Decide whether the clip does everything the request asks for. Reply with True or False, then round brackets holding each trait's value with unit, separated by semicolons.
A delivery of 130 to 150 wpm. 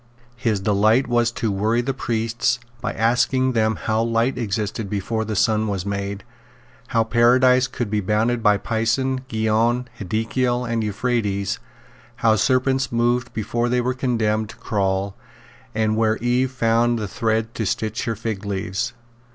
True (145 wpm)